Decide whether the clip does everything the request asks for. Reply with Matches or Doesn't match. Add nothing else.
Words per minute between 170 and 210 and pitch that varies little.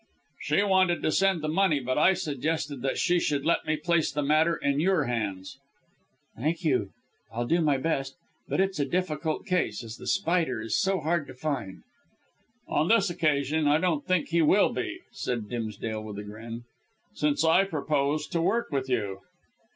Doesn't match